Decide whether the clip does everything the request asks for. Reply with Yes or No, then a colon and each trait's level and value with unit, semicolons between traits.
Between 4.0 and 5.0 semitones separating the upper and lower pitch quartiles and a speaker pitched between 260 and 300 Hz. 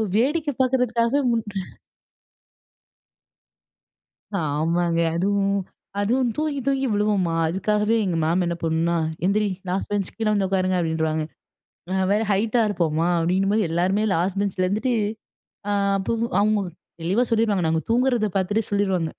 No: average, 4.3 semitones; high, 200 Hz